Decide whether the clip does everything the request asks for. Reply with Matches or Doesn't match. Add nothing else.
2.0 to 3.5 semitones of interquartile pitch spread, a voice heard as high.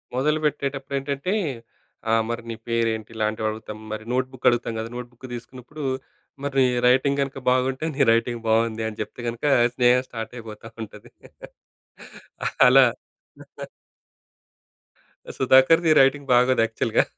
Doesn't match